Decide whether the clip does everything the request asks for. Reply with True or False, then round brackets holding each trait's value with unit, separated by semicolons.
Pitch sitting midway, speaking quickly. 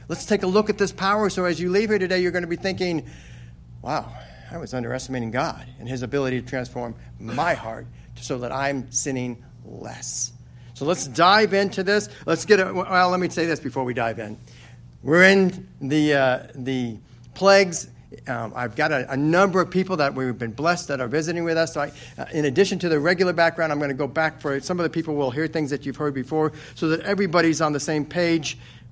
True (150 Hz; 225 wpm)